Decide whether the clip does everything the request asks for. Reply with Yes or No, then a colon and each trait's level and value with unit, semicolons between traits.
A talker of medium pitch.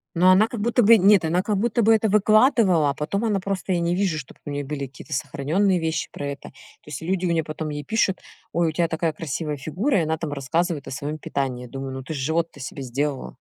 Yes: medium, 165 Hz